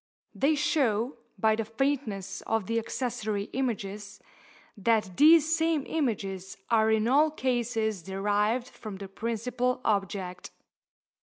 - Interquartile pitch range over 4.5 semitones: No, average, 4.0 semitones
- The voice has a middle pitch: No, high, 225 Hz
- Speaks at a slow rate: Yes, slow, 120 wpm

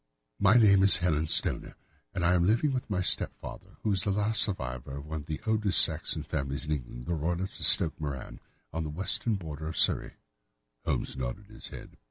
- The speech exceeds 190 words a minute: Yes, fast, 205 wpm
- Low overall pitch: Yes, very low, 85 Hz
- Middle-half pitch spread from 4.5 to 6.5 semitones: Yes, average, 5.1 semitones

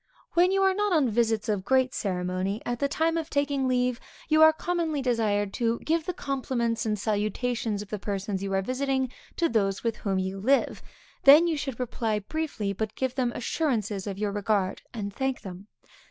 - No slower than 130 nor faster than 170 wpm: No, average, 195 wpm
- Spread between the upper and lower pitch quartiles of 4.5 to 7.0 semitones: Yes, wide, 5.4 semitones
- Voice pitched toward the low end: No, high, 235 Hz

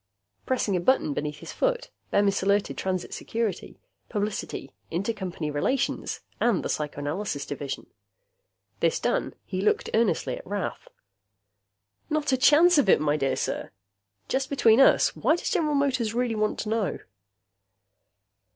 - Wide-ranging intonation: Yes, wide, 6.7 semitones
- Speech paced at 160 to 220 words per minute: No, average, 140 wpm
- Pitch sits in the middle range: No, high, 210 Hz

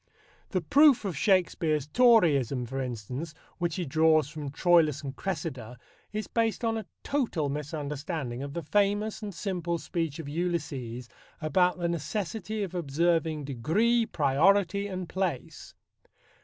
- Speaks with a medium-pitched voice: Yes, medium, 165 Hz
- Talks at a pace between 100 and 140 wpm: Yes, slow, 135 wpm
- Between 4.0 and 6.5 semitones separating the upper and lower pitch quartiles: Yes, average, 5.3 semitones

